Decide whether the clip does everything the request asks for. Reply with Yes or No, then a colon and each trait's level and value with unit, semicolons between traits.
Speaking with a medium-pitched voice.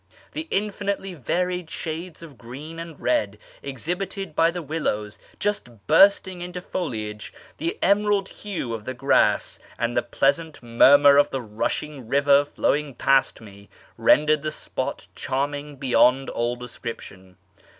Yes: medium, 145 Hz